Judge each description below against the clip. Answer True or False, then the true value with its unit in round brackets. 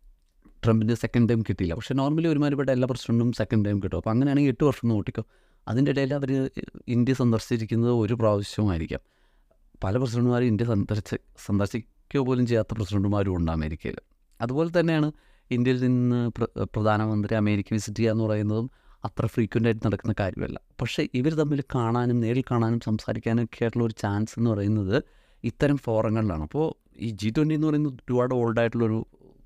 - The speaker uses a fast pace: True (140 wpm)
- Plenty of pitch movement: False (3.1 semitones)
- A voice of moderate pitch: False (115 Hz)